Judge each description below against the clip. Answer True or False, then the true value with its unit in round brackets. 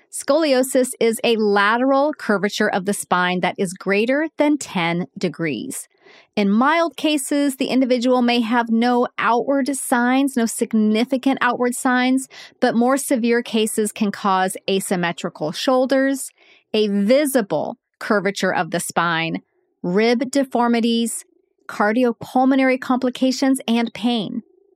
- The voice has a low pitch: False (245 Hz)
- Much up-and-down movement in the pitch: False (4.5 semitones)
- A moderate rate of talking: False (115 wpm)